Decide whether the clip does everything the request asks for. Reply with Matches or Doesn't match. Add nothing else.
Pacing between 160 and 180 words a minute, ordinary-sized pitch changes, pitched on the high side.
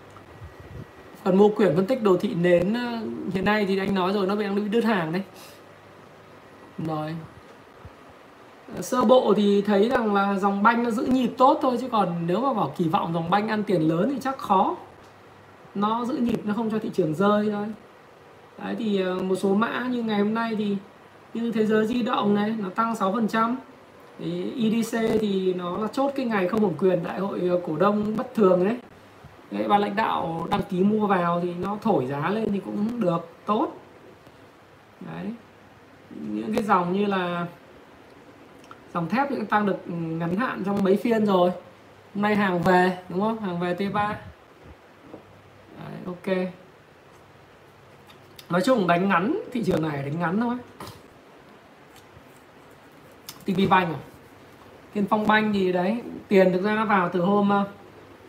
Matches